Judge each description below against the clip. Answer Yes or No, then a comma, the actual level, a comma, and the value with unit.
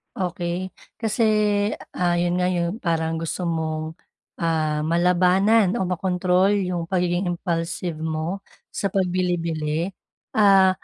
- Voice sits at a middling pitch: Yes, medium, 175 Hz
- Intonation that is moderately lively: No, narrow, 2.0 semitones